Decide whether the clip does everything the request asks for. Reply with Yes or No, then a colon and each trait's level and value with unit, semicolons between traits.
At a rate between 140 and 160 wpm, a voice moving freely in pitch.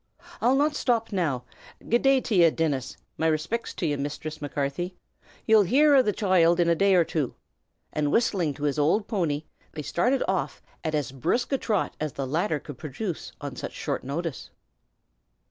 No: average, 185 wpm; wide, 6.4 semitones